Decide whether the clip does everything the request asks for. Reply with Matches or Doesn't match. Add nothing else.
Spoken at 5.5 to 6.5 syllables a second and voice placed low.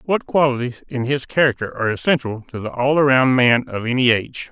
Matches